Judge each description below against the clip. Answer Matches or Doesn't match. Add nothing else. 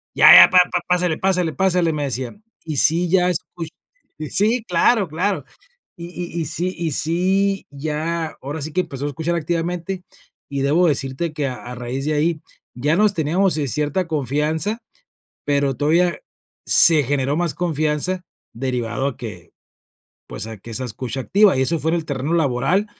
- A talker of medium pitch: Matches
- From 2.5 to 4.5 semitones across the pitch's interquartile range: Matches